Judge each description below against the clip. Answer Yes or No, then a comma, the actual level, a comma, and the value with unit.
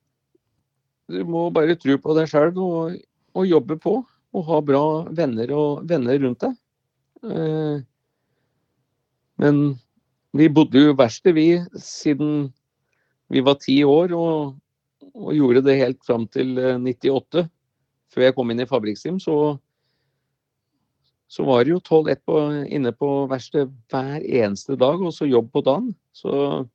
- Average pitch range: Yes, average, 3.0 semitones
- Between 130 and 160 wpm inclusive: Yes, average, 135 wpm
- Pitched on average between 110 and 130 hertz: No, medium, 140 Hz